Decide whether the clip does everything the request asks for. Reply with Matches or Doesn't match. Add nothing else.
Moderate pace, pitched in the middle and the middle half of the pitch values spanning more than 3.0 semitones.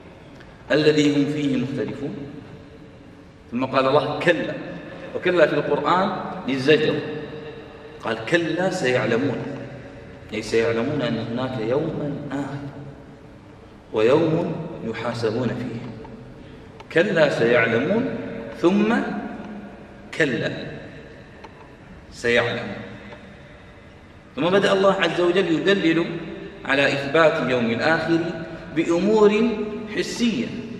Matches